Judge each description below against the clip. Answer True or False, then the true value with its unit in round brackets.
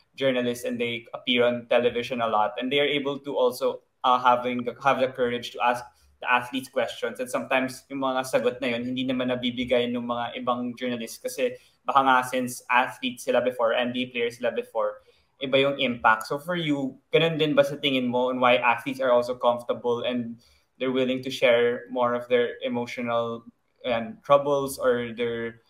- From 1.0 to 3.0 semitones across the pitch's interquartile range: True (2.7 semitones)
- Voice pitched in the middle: False (125 Hz)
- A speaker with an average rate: False (185 wpm)